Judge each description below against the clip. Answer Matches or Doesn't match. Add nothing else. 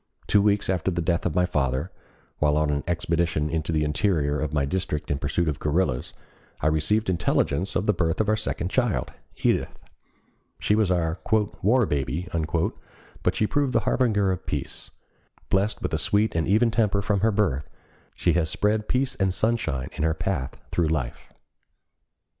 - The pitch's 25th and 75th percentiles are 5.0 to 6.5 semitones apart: Matches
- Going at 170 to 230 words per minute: Matches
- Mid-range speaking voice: Doesn't match